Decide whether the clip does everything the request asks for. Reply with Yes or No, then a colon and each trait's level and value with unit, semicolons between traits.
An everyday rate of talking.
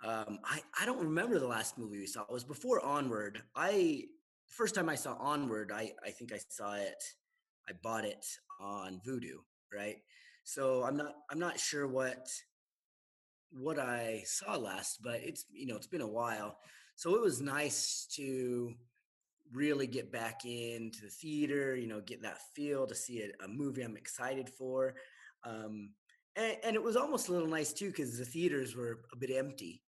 Yes: average, 185 wpm